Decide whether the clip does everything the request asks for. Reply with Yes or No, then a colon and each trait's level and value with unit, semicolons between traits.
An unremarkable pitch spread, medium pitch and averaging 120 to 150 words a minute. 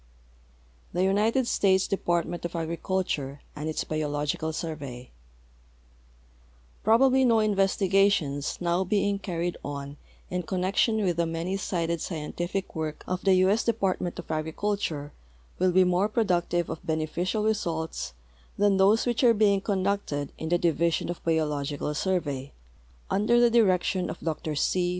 Yes: average, 4.0 semitones; medium, 180 Hz; average, 140 wpm